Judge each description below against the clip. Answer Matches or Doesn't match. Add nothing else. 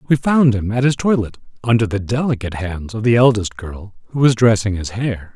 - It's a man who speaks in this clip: Matches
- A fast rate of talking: Matches